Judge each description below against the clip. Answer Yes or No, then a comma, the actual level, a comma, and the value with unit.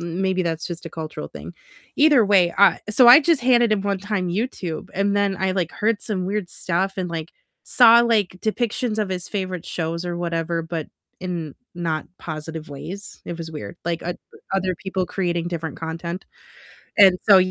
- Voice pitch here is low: No, medium, 185 Hz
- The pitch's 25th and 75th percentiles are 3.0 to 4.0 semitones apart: Yes, average, 3.3 semitones